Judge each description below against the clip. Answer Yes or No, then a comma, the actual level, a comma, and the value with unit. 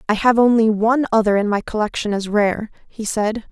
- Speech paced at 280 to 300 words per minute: No, fast, 205 wpm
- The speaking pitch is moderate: No, high, 215 Hz